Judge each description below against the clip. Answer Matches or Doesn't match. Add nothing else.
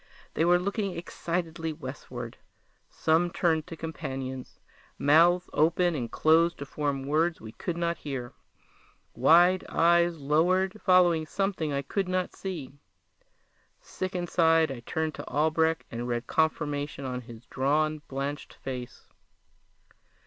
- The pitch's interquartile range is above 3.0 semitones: Matches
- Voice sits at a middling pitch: Matches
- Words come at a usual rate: Doesn't match